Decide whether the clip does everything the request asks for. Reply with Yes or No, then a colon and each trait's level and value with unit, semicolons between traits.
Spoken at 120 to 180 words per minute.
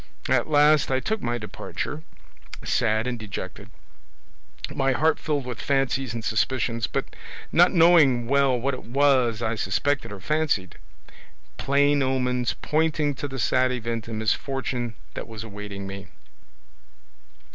Yes: slow, 135 wpm